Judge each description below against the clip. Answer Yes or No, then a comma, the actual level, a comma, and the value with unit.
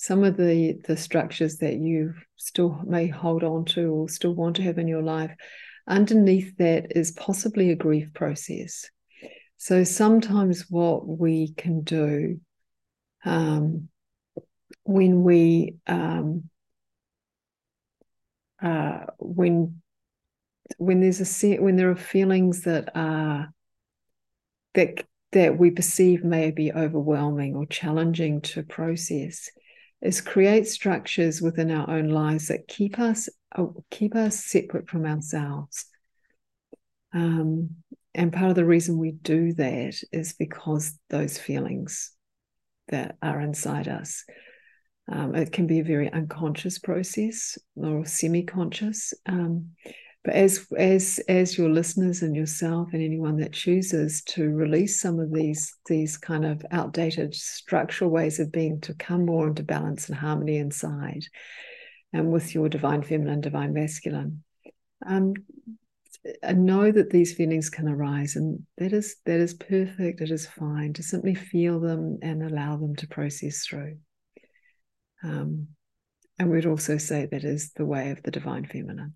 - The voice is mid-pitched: Yes, medium, 165 Hz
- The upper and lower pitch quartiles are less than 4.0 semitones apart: Yes, average, 2.9 semitones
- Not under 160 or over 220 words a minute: No, average, 140 wpm